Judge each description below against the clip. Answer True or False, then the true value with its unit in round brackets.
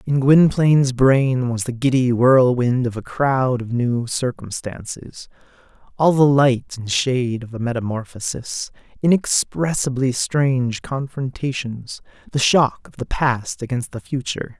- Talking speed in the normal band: False (130 wpm)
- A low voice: True (130 Hz)